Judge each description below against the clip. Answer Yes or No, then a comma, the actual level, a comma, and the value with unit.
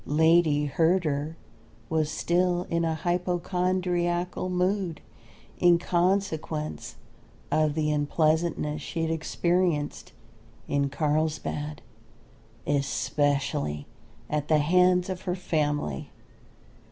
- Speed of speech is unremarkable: No, slow, 90 wpm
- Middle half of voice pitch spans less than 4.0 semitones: Yes, average, 3.1 semitones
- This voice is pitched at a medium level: Yes, medium, 160 Hz